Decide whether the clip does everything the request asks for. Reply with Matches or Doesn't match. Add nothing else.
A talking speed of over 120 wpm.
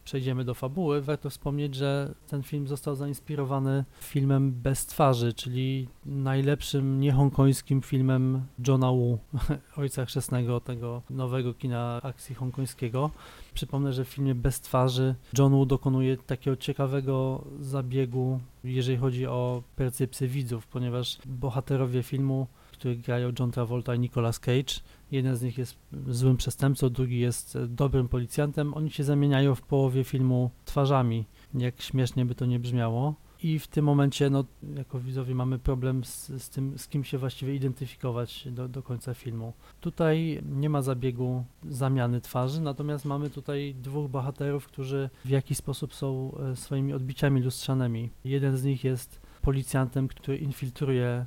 Matches